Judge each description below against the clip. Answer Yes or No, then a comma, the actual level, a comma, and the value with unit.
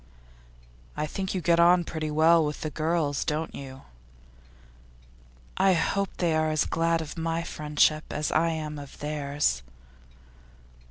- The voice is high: No, medium, 155 Hz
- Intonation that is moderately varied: No, narrow, 2.0 semitones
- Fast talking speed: No, average, 145 wpm